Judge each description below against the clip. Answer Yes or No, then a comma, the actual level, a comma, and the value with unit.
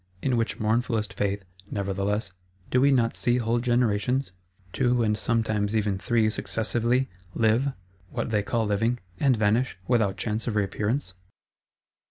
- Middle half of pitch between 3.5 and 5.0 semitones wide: No, average, 2.9 semitones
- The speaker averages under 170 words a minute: Yes, slow, 135 wpm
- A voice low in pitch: Yes, low, 115 Hz